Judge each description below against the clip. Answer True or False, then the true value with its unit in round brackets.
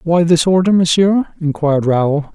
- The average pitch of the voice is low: False (165 Hz)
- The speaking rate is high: False (155 wpm)